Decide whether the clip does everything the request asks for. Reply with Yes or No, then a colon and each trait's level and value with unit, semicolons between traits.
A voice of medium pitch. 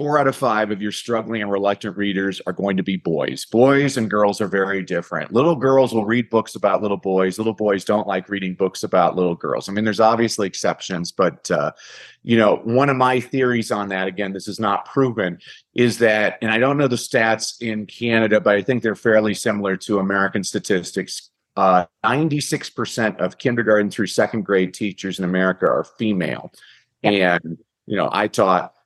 No: low, 105 Hz